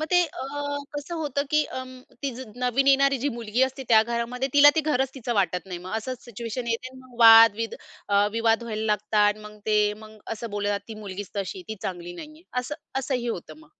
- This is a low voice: No, high, 235 Hz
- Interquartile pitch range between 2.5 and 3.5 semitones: No, average, 4.0 semitones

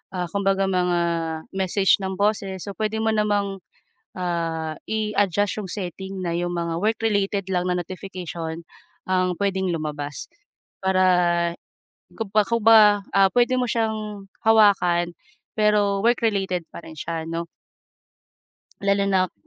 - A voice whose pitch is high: Yes, high, 195 Hz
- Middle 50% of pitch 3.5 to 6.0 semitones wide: No, average, 3.0 semitones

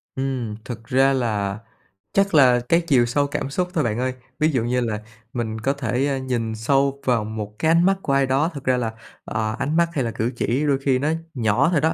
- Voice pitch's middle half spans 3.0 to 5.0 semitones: Yes, average, 3.7 semitones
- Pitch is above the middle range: No, low, 130 Hz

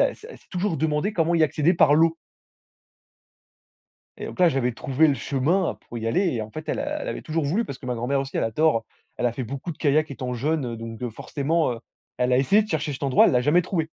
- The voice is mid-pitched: Yes, medium, 145 Hz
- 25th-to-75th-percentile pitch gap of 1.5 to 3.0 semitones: No, average, 4.7 semitones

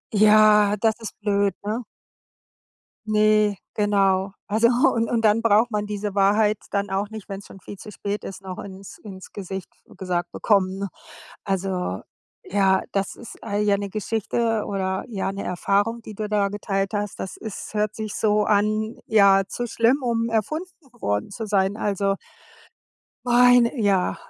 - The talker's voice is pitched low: No, high, 205 Hz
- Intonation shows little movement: Yes, narrow, 1.9 semitones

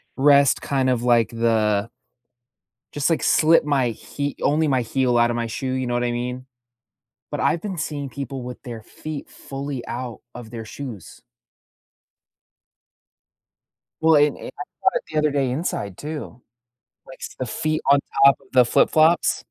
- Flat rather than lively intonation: No, average, 3.3 semitones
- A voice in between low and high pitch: No, low, 130 Hz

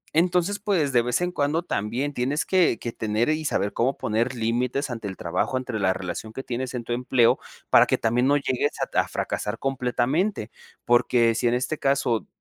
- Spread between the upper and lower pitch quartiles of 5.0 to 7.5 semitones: No, average, 3.8 semitones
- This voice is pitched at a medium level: No, low, 125 Hz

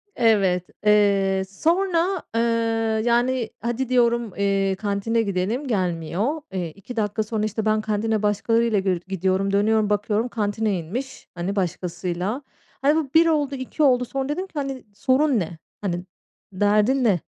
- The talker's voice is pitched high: Yes, high, 215 Hz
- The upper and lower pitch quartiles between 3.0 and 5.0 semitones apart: Yes, average, 4.2 semitones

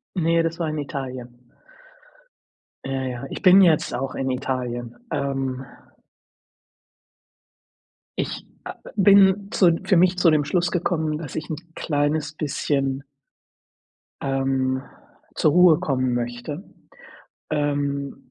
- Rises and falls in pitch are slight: No, average, 3.9 semitones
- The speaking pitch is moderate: Yes, medium, 145 Hz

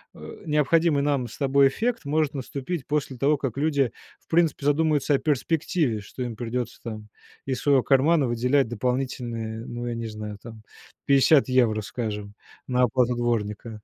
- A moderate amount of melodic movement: Yes, average, 3.7 semitones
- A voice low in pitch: Yes, low, 130 Hz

